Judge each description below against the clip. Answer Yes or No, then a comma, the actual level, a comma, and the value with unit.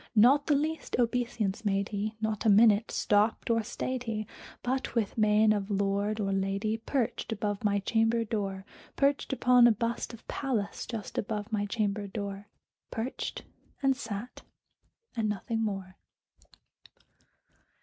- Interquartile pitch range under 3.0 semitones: Yes, narrow, 2.5 semitones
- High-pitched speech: Yes, high, 215 Hz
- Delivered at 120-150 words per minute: Yes, average, 140 wpm